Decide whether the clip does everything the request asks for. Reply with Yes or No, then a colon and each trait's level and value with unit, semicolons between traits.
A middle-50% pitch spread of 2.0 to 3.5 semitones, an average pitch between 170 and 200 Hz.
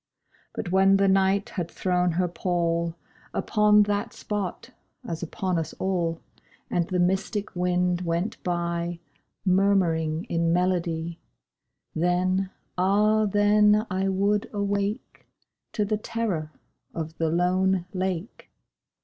Yes: average, 2.7 semitones; medium, 185 Hz